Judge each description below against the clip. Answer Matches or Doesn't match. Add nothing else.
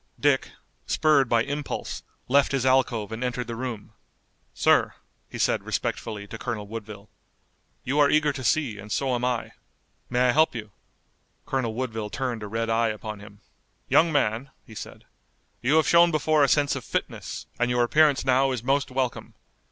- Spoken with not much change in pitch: Doesn't match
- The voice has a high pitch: Doesn't match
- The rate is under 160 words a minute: Doesn't match